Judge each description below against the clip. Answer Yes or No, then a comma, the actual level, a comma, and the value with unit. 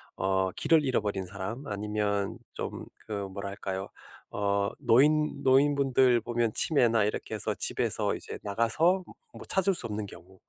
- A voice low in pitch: Yes, low, 105 Hz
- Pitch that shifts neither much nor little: Yes, average, 4.9 semitones